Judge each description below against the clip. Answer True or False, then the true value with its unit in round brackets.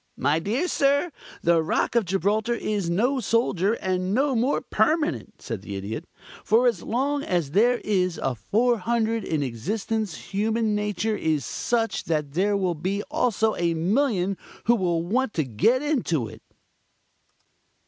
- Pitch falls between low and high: False (210 Hz)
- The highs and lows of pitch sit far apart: True (5.8 semitones)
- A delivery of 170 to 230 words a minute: False (150 wpm)